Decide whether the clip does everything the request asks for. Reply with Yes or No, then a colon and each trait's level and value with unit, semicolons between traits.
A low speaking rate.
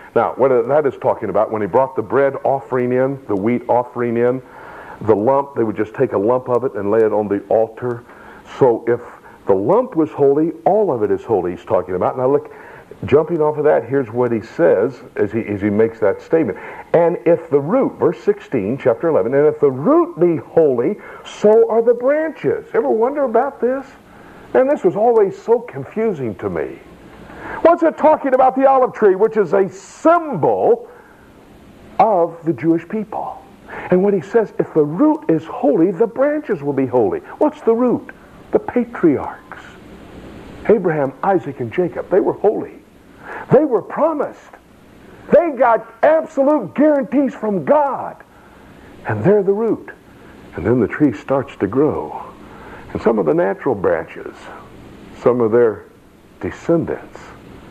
No: average, 170 wpm